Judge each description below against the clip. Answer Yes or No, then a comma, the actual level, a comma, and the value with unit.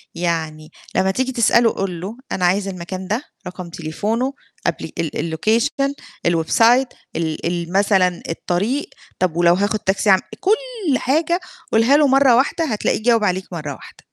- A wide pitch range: Yes, wide, 6.6 semitones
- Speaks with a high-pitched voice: Yes, high, 200 Hz